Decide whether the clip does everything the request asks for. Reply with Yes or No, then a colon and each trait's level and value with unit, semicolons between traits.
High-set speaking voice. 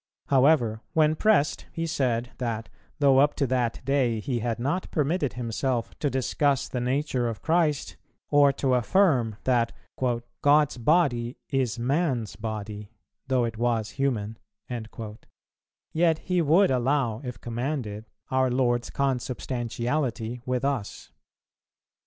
No: low, 130 Hz